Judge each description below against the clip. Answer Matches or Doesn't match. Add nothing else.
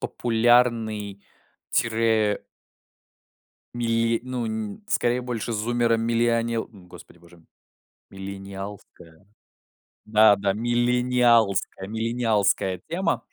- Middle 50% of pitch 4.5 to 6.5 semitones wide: Doesn't match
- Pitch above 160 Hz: Doesn't match